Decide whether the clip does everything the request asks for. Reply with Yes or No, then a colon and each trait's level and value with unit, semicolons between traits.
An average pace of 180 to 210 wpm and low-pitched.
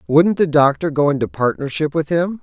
No: average, 200 wpm; medium, 145 Hz